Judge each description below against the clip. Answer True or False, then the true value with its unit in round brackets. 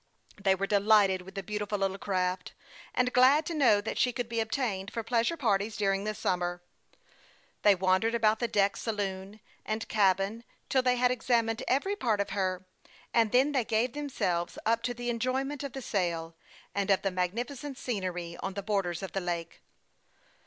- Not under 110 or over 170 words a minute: False (185 wpm)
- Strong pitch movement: False (4.1 semitones)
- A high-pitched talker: True (210 Hz)